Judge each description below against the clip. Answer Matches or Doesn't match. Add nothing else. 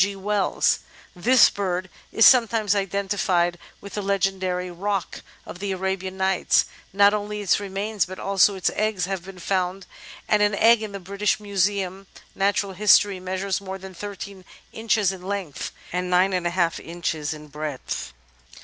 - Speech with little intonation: Matches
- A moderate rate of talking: Matches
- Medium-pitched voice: Doesn't match